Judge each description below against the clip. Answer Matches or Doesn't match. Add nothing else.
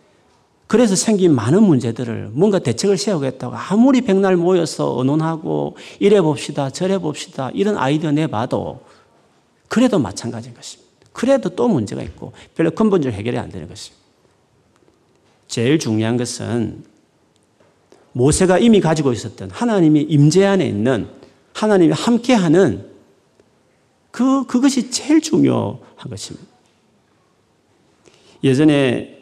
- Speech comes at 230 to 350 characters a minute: Matches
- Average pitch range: Doesn't match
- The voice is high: Doesn't match